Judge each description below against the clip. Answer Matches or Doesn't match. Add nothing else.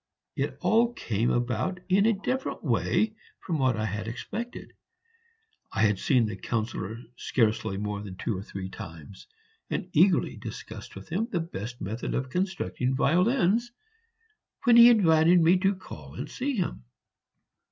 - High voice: Doesn't match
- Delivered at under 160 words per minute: Matches